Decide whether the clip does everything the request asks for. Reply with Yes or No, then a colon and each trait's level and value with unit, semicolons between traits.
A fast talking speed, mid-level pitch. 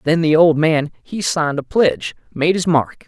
Yes: fast, 215 wpm; medium, 160 Hz